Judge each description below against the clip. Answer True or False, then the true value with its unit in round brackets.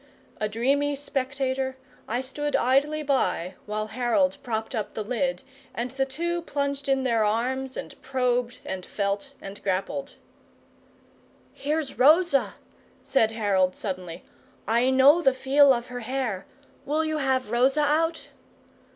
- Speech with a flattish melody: False (3.8 semitones)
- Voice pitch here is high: True (260 Hz)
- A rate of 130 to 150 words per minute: True (135 wpm)